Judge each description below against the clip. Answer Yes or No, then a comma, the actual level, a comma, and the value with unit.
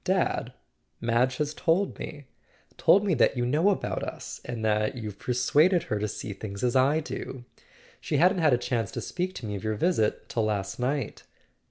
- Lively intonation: Yes, wide, 6.6 semitones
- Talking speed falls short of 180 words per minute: No, average, 190 wpm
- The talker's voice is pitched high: No, low, 125 Hz